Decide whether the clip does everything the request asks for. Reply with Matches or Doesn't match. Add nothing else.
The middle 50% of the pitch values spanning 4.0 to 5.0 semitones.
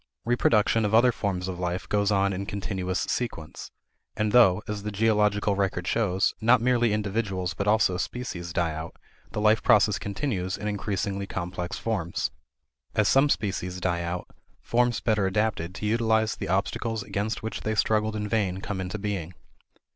Doesn't match